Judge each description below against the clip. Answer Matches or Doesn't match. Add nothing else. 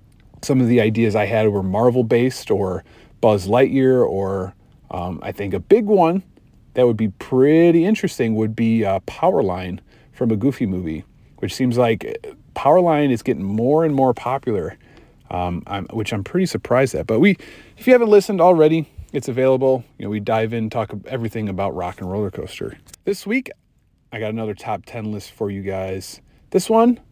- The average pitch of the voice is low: Matches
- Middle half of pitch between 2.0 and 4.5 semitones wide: Doesn't match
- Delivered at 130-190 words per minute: Matches